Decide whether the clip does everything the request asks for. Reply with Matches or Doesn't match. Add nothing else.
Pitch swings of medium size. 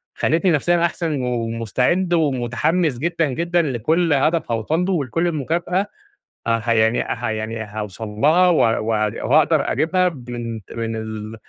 Doesn't match